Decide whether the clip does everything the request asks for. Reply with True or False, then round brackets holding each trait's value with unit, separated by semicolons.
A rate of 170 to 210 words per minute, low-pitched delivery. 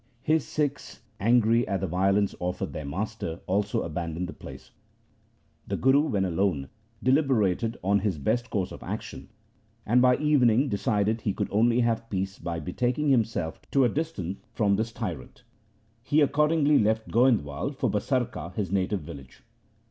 False (155 wpm; 110 Hz)